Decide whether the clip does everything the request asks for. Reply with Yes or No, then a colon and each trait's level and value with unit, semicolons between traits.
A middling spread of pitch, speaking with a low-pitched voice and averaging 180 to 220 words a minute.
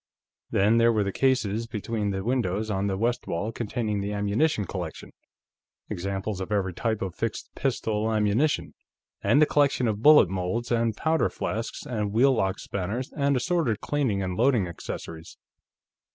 No: average, 3.6 semitones; low, 110 Hz; average, 160 wpm